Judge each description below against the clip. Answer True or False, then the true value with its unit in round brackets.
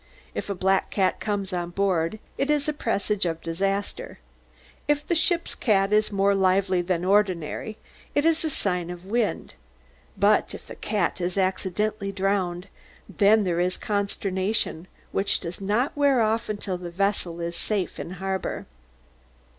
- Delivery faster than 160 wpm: False (155 wpm)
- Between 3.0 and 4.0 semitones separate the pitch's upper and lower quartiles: False (2.6 semitones)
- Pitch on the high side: True (195 Hz)